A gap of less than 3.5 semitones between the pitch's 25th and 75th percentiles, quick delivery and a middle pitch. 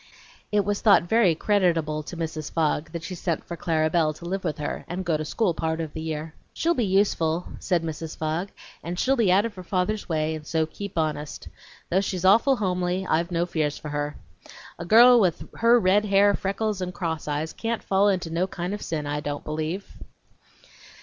No: average, 3.8 semitones; fast, 210 wpm; medium, 175 Hz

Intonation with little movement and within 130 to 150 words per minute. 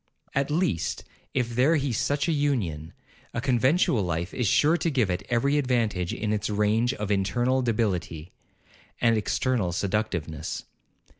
No: wide, 5.5 semitones; average, 145 wpm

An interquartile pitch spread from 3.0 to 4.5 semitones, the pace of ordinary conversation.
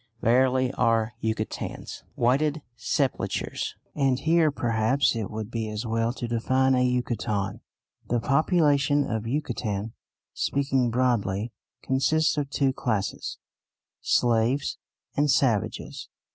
No: average, 3.5 semitones; slow, 110 wpm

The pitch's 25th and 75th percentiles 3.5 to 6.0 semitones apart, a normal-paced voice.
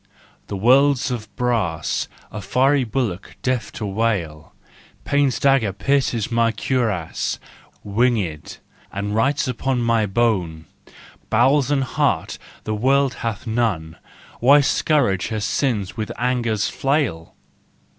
No: average, 4.6 semitones; slow, 125 wpm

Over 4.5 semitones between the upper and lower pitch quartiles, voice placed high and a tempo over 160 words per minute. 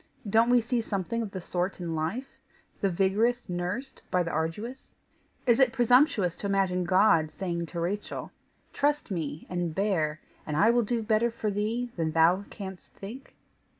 Yes: average, 5.1 semitones; high, 195 Hz; average, 170 wpm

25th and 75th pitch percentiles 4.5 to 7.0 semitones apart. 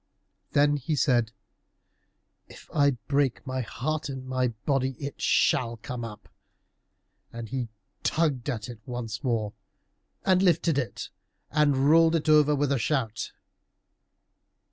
No: average, 3.6 semitones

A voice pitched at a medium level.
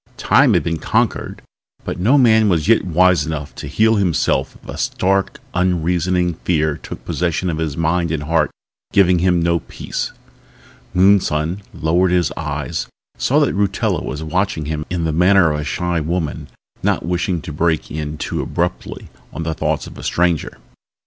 No: very low, 85 Hz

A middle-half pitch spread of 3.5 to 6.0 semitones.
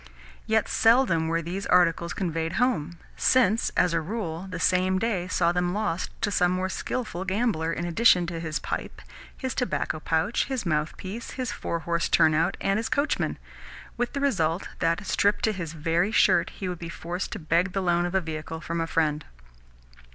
Yes: average, 3.8 semitones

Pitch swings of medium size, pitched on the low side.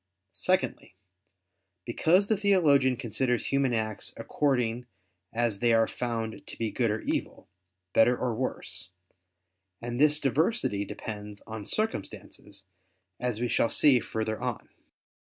Yes: average, 3.8 semitones; low, 120 Hz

